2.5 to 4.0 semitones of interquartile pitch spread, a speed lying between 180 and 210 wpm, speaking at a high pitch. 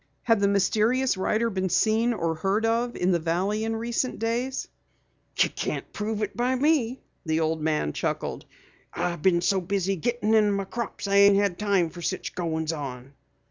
No: average, 4.6 semitones; average, 185 wpm; high, 200 Hz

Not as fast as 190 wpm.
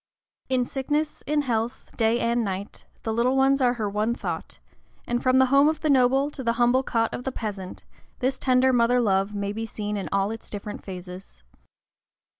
No: average, 195 wpm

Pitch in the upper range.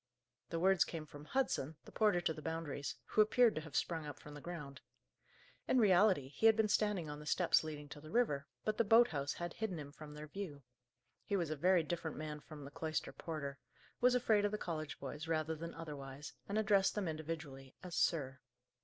No: medium, 160 Hz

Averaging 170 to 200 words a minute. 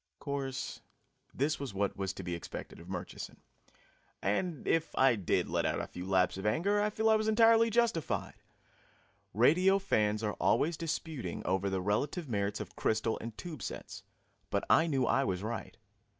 Yes: average, 180 wpm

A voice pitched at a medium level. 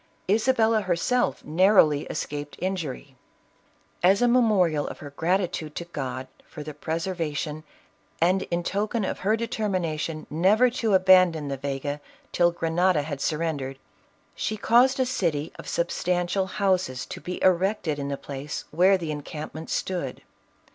Yes: medium, 170 Hz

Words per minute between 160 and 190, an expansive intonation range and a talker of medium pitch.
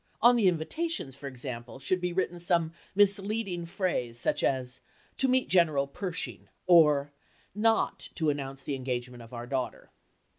No: average, 150 wpm; wide, 6.2 semitones; medium, 160 Hz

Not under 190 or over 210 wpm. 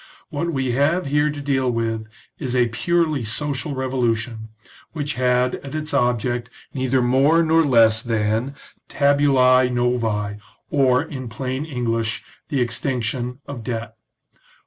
No: slow, 135 wpm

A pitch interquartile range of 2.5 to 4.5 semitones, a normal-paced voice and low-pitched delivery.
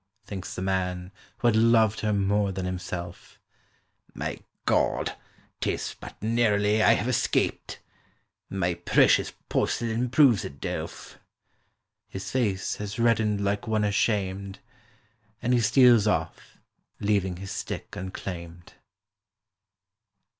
No: average, 2.9 semitones; slow, 110 wpm; low, 100 Hz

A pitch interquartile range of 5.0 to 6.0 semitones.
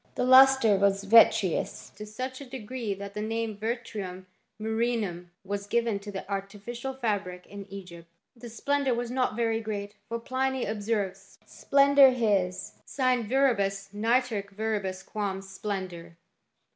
No: average, 3.4 semitones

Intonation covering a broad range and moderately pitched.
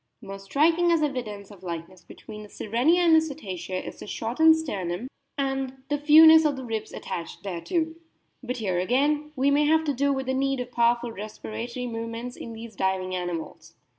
No: wide, 6.3 semitones; high, 245 Hz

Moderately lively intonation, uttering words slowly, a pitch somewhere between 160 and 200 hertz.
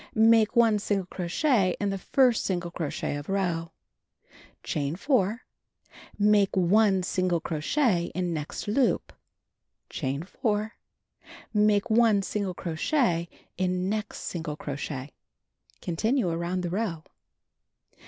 Yes: average, 4.0 semitones; slow, 115 wpm; high, 190 Hz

